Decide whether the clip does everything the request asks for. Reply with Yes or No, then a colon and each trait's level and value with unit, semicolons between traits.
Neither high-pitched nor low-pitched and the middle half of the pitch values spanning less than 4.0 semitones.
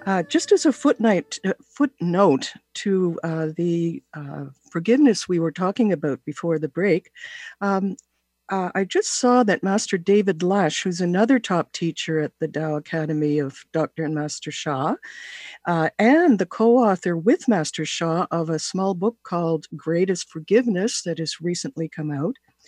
No: medium, 180 Hz; average, 4.6 semitones